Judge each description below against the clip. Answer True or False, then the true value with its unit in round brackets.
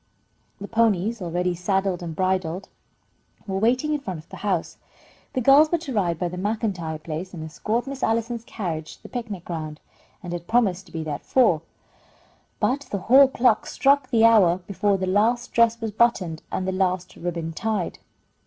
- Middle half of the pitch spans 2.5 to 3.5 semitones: False (4.9 semitones)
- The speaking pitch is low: False (195 Hz)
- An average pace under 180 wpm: False (185 wpm)